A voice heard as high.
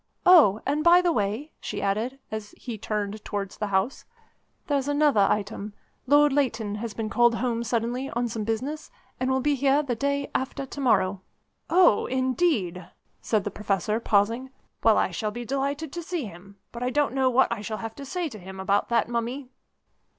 Yes: high, 235 Hz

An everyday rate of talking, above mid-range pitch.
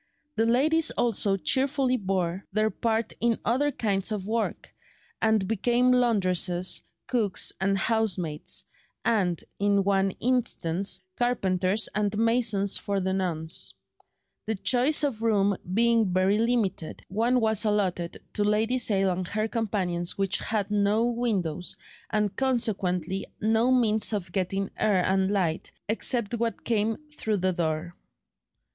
No: slow, 130 wpm; high, 210 Hz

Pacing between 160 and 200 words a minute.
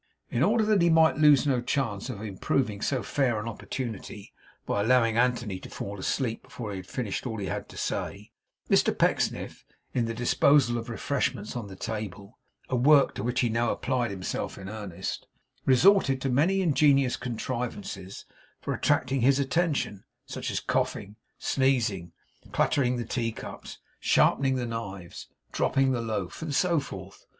Yes: average, 165 wpm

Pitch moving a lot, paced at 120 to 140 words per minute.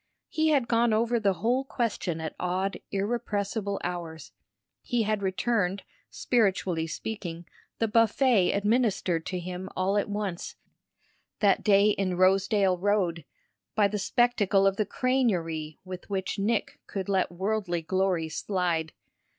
No: average, 3.3 semitones; slow, 135 wpm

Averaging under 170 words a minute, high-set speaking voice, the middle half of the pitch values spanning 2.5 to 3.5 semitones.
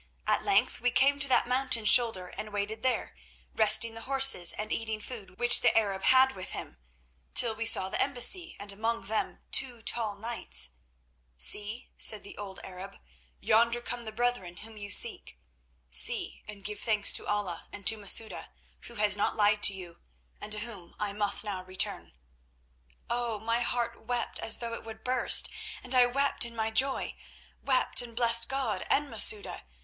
No: average, 175 wpm; high, 220 Hz; average, 3.0 semitones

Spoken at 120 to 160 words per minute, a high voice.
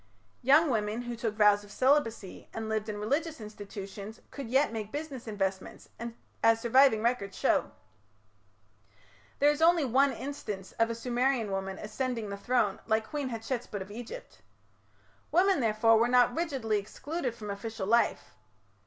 Yes: average, 150 wpm; high, 230 Hz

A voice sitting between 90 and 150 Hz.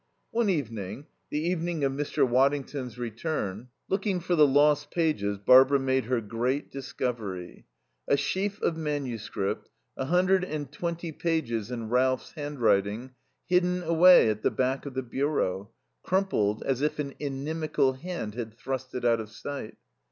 Yes: low, 135 Hz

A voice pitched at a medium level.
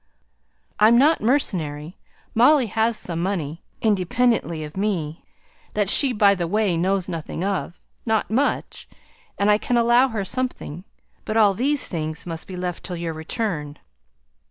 No: high, 200 Hz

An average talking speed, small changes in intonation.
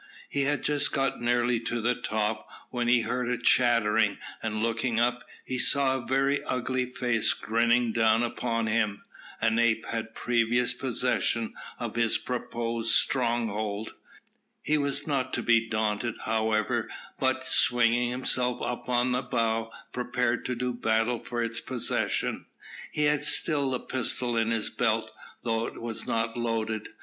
Yes: average, 150 wpm; narrow, 1.7 semitones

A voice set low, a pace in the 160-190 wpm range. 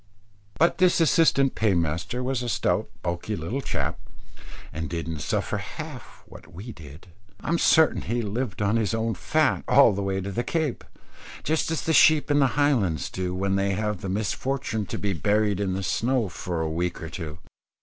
Yes: low, 105 Hz; average, 185 wpm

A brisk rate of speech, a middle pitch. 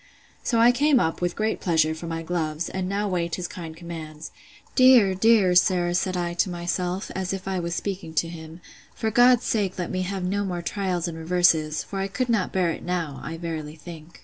Yes: fast, 215 wpm; medium, 180 Hz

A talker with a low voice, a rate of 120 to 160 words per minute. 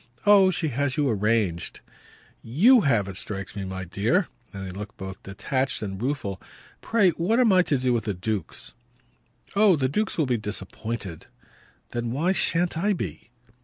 No: low, 120 Hz; average, 170 wpm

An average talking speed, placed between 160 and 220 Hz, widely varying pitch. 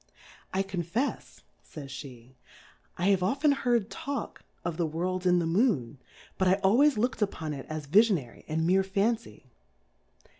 Yes: average, 150 wpm; medium, 185 Hz; wide, 5.8 semitones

